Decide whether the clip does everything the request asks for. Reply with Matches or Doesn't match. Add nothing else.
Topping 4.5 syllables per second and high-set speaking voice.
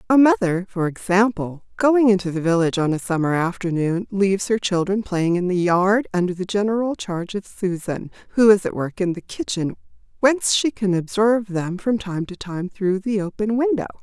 Matches